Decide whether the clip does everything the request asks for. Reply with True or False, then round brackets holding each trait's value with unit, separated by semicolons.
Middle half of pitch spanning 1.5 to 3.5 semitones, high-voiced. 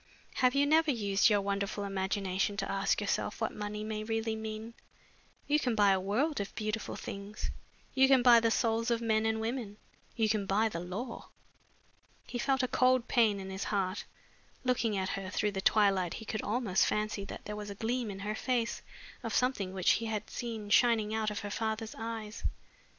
True (2.5 semitones; 215 Hz)